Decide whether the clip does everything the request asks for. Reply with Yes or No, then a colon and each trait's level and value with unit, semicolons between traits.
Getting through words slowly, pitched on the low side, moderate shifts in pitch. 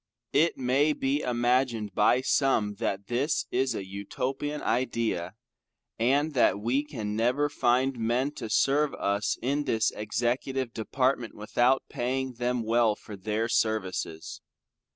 Yes: slow, 130 wpm; low, 120 Hz; average, 3.5 semitones